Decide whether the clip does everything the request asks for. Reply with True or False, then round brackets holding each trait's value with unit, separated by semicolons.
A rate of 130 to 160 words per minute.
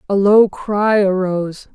True (140 wpm)